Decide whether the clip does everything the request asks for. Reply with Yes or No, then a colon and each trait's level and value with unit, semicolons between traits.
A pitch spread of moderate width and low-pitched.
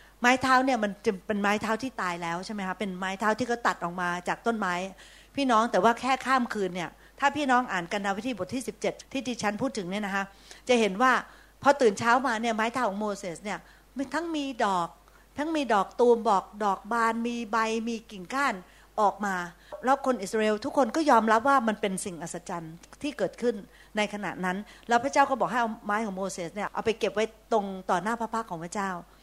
No: average, 4.2 semitones; high, 220 Hz